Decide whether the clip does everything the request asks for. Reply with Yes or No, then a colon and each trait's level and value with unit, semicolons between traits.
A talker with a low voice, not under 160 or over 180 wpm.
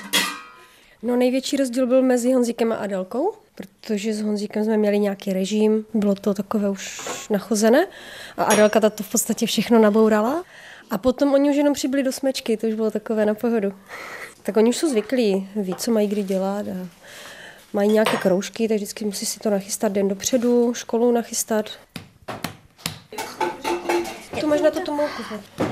No: high, 220 Hz; average, 165 wpm